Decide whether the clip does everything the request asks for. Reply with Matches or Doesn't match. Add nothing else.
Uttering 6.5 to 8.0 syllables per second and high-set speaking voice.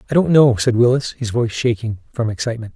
Doesn't match